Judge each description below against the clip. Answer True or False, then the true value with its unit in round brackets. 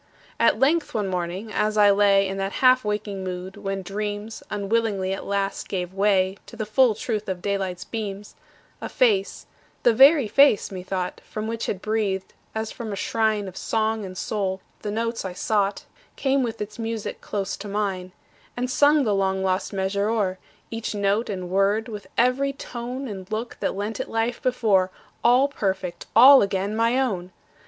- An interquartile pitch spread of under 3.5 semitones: True (2.9 semitones)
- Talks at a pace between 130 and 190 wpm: True (180 wpm)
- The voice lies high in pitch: True (210 Hz)